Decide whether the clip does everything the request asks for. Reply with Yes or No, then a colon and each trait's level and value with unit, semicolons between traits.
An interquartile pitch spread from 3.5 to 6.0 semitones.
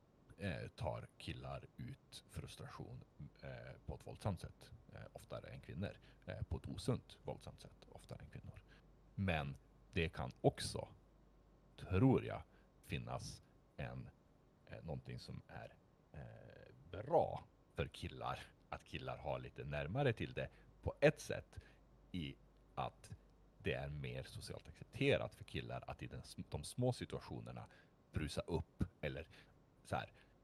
Yes: average, 5.3 semitones